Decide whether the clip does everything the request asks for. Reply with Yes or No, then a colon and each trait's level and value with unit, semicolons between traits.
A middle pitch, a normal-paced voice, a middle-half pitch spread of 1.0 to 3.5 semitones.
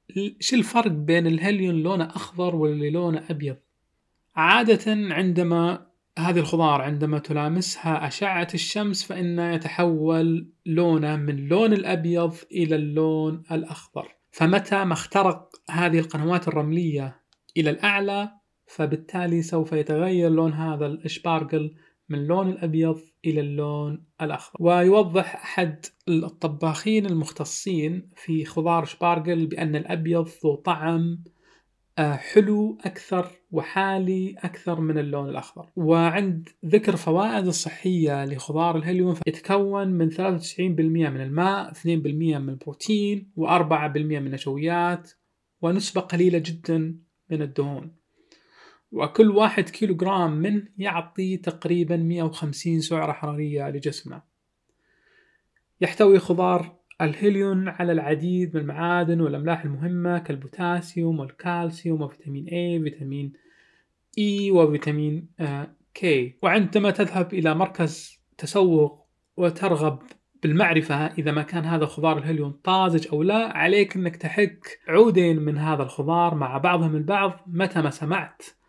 Yes: medium, 170 Hz; average, 110 wpm; average, 2.7 semitones